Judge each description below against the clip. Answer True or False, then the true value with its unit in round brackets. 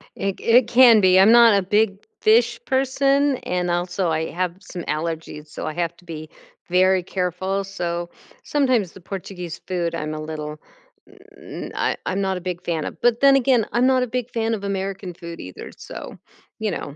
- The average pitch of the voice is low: False (190 Hz)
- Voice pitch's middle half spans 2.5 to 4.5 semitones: False (4.9 semitones)